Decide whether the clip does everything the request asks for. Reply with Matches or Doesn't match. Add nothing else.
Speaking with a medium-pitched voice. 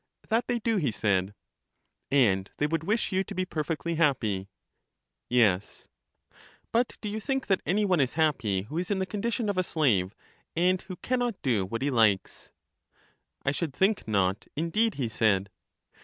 Matches